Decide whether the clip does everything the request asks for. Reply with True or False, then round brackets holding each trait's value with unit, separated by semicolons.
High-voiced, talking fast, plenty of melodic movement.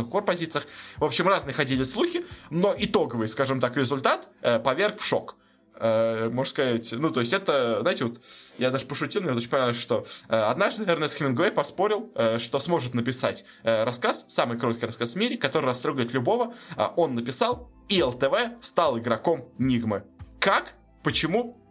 False (140 Hz; 170 wpm; 6.9 semitones)